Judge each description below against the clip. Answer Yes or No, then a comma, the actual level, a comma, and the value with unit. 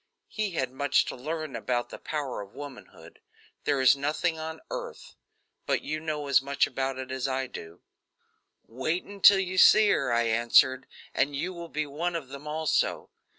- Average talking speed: Yes, average, 180 wpm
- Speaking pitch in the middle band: Yes, medium, 145 Hz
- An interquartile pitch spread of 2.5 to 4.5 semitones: Yes, average, 3.8 semitones